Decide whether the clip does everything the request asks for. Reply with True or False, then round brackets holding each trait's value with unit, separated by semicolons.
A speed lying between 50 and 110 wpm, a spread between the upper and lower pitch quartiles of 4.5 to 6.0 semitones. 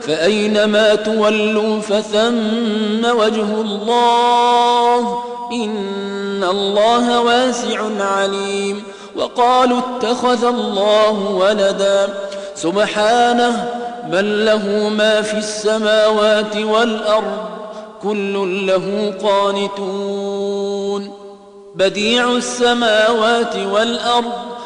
False (65 wpm; 2.9 semitones)